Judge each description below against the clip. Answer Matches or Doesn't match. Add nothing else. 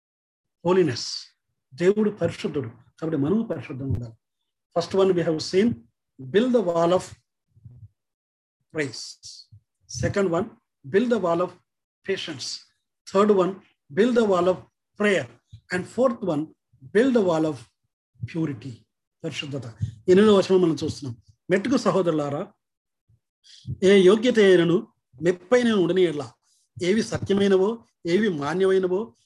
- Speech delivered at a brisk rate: Doesn't match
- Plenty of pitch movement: Matches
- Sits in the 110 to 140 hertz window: Doesn't match